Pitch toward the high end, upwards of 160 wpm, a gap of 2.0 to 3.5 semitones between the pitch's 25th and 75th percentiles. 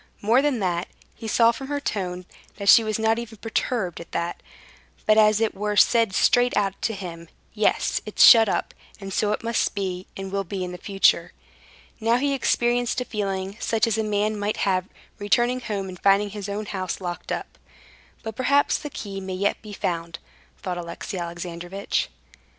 Yes: high, 205 Hz; average, 185 wpm; average, 3.2 semitones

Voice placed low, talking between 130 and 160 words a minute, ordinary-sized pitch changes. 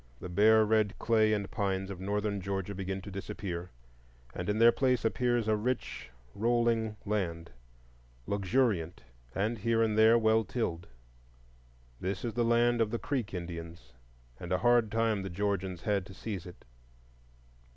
Yes: low, 105 Hz; average, 155 wpm; average, 3.2 semitones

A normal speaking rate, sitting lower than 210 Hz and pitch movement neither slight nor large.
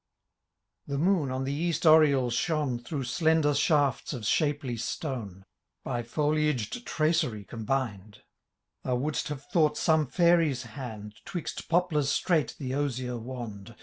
No: slow, 130 wpm; medium, 140 Hz; average, 4.2 semitones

